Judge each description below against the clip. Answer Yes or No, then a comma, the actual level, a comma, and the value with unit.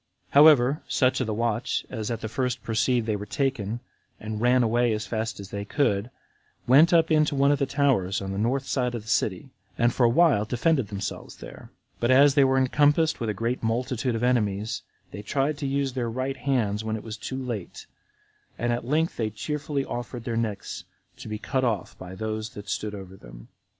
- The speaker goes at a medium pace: No, fast, 210 wpm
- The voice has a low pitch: Yes, low, 120 Hz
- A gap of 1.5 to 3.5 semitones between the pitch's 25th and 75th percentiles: No, average, 3.9 semitones